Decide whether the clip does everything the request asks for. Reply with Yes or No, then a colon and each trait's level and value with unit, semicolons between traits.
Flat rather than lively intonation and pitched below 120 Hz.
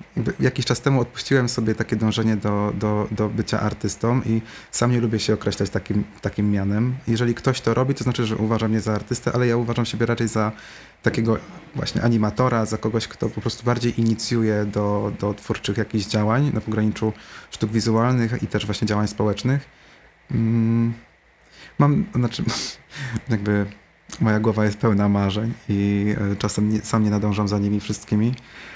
Yes: narrow, 1.9 semitones; low, 110 Hz